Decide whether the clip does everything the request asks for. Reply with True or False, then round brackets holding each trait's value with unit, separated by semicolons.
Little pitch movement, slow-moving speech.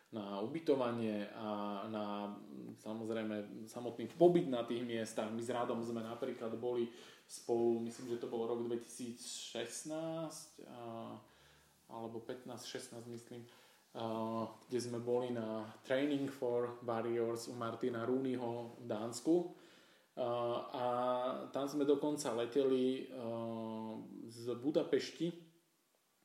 True (1.9 semitones; 105 wpm)